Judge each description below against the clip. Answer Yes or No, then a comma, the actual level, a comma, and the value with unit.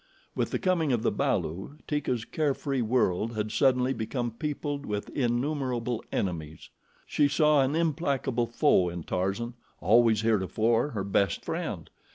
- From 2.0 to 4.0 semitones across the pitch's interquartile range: No, average, 4.8 semitones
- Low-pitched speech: Yes, low, 120 Hz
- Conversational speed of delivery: Yes, average, 145 wpm